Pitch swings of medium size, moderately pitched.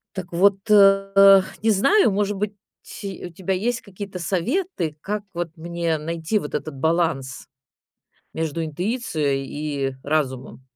Yes: average, 4.0 semitones; medium, 180 Hz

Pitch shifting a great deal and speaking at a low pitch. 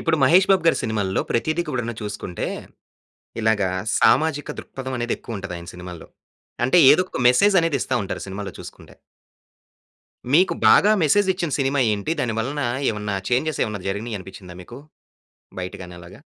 Yes: wide, 7.8 semitones; low, 120 Hz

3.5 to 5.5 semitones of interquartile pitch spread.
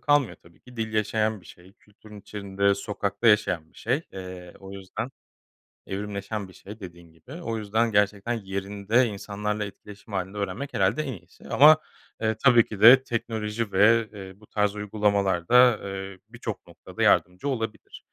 No: narrow, 2.6 semitones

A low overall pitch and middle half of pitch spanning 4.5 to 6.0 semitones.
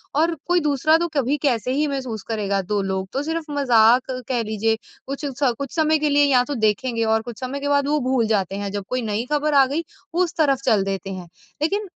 No: very high, 260 Hz; average, 5.1 semitones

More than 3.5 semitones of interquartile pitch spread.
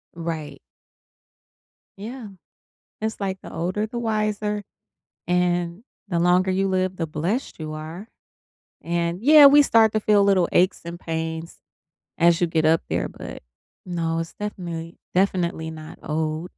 Yes: average, 3.9 semitones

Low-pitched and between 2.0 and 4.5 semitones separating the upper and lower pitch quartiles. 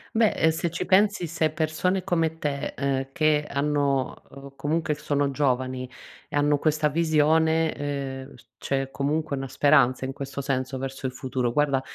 No: medium, 145 Hz; average, 2.7 semitones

